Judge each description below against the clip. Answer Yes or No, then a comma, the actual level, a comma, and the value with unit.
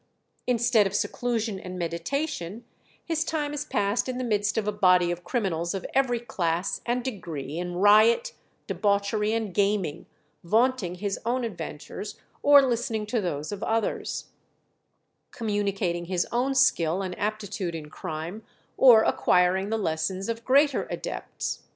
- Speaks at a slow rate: No, average, 145 wpm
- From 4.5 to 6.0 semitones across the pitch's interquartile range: Yes, average, 4.9 semitones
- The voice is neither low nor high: No, high, 205 Hz